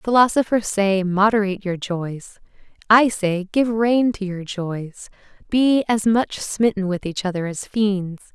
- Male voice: No, female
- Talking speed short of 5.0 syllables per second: Yes, 4.0 syllables/s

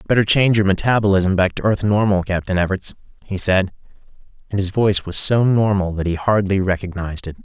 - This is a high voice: No, very low, 95 Hz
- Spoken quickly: No, average, 185 wpm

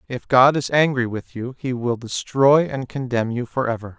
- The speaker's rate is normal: Yes, average, 195 wpm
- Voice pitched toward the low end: Yes, low, 125 Hz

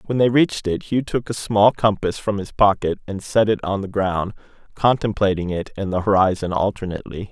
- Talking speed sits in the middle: Yes, average, 195 wpm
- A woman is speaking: No, male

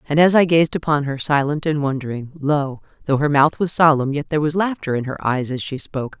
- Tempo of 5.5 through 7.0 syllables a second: Yes, 5.8 syllables/s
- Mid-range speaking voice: Yes, medium, 145 Hz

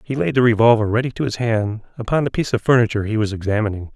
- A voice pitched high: No, low, 115 Hz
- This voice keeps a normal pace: No, fast, 240 wpm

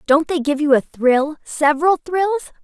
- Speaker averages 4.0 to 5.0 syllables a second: Yes, 4.5 syllables/s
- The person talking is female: Yes, female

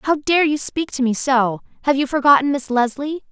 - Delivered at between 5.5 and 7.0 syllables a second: No, 5.0 syllables/s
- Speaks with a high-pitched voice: Yes, very high, 275 Hz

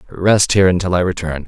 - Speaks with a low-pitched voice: Yes, very low, 90 Hz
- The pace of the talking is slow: No, fast, 205 wpm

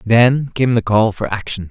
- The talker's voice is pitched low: Yes, low, 110 Hz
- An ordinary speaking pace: No, fast, 210 wpm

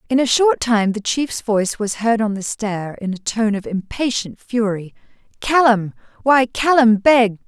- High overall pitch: Yes, high, 225 Hz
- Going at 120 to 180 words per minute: Yes, average, 175 wpm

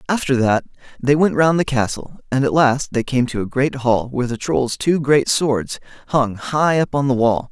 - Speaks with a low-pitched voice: Yes, low, 130 Hz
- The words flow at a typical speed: No, fast, 225 wpm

